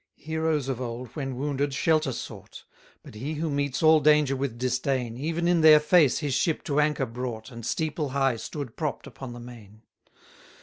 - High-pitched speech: No, medium, 140 Hz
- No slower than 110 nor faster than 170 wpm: No, average, 185 wpm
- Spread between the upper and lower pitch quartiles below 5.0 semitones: Yes, average, 3.6 semitones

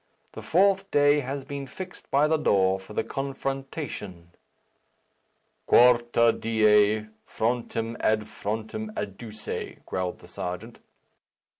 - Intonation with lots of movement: No, average, 4.6 semitones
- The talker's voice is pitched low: Yes, low, 115 Hz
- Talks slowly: Yes, slow, 110 wpm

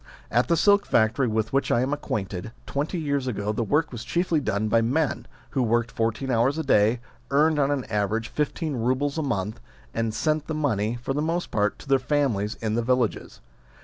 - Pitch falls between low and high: No, low, 125 Hz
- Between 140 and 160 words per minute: No, fast, 205 wpm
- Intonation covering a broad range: No, average, 4.8 semitones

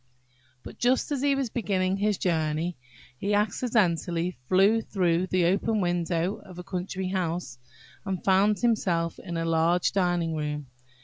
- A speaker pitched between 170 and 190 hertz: Yes, medium, 185 Hz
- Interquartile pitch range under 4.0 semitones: Yes, average, 3.3 semitones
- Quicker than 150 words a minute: No, average, 145 wpm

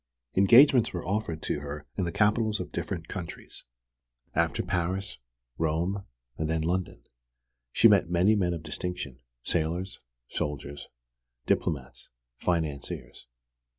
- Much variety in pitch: No, average, 3.9 semitones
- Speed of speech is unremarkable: No, slow, 120 wpm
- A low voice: Yes, very low, 85 Hz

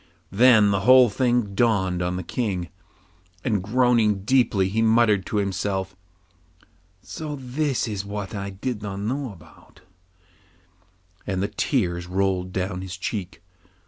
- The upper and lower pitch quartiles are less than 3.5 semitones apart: No, average, 4.0 semitones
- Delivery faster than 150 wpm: No, slow, 135 wpm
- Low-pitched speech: Yes, low, 100 Hz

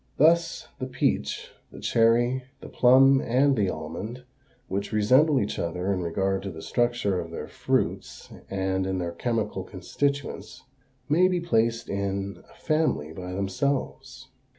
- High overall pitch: No, low, 110 Hz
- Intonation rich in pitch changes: Yes, wide, 5.8 semitones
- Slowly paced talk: No, average, 145 wpm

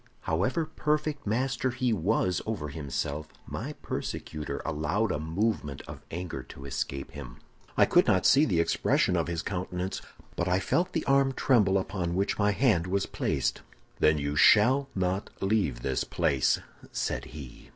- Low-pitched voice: Yes, very low, 95 Hz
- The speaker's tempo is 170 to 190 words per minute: No, average, 160 wpm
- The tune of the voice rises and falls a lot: Yes, wide, 6.5 semitones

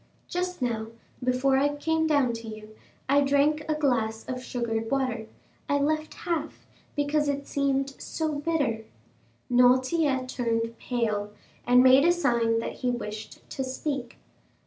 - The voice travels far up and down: No, average, 3.7 semitones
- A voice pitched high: Yes, very high, 260 Hz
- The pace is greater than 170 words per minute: No, average, 145 wpm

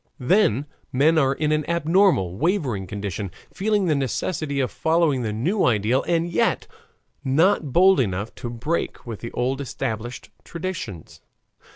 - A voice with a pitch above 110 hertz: Yes, medium, 140 Hz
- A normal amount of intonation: No, wide, 6.4 semitones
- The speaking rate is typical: Yes, average, 145 wpm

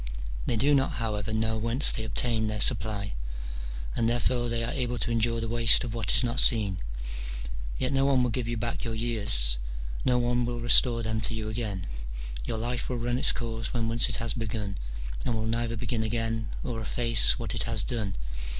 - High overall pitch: No, low, 115 Hz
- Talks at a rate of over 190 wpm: Yes, fast, 205 wpm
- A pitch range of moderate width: No, narrow, 1.6 semitones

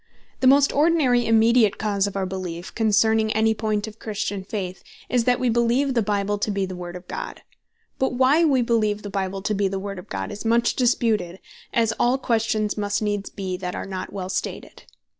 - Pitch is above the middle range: Yes, high, 215 Hz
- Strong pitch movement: No, average, 3.3 semitones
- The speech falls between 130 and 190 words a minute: No, fast, 205 wpm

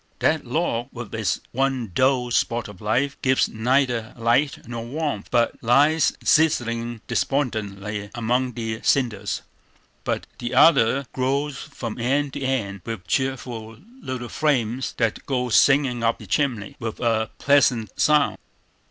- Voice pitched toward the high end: No, low, 120 Hz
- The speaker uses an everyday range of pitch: Yes, average, 3.2 semitones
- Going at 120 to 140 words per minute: Yes, slow, 135 wpm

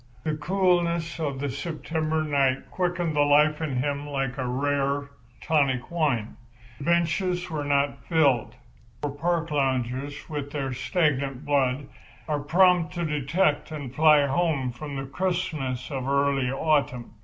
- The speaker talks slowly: No, average, 145 wpm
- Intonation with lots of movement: No, average, 2.9 semitones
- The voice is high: No, medium, 145 Hz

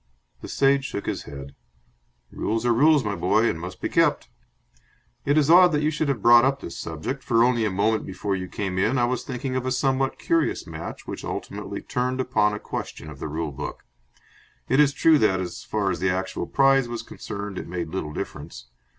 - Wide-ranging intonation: Yes, wide, 6.3 semitones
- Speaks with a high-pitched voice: No, low, 115 Hz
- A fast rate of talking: Yes, fast, 210 wpm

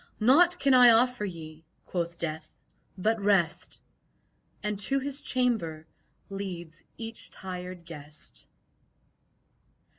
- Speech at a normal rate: No, slow, 100 wpm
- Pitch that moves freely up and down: Yes, wide, 6.1 semitones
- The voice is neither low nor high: No, high, 195 Hz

